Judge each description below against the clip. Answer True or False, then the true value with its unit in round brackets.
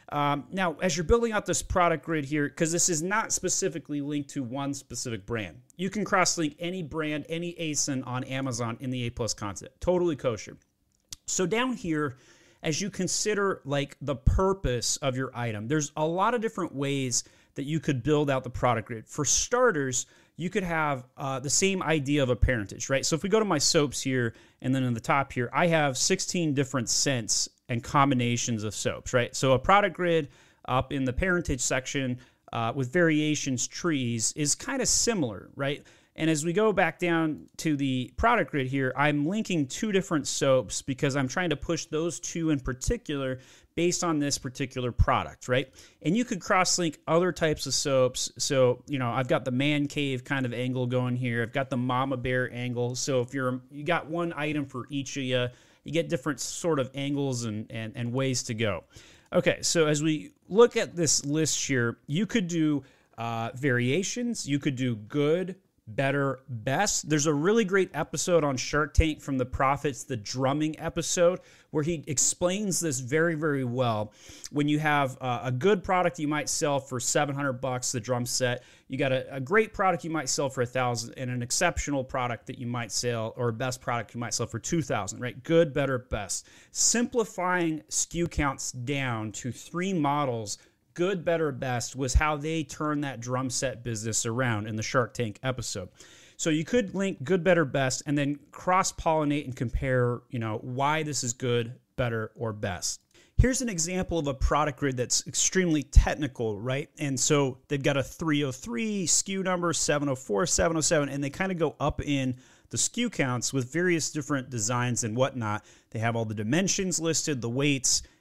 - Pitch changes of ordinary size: True (4.5 semitones)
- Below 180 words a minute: False (190 wpm)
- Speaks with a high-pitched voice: False (140 Hz)